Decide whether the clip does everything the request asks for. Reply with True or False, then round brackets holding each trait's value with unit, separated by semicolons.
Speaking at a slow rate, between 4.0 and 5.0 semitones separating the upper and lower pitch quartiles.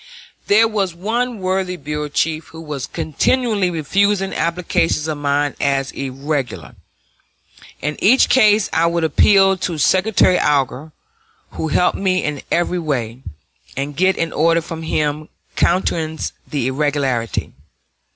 True (130 wpm; 4.4 semitones)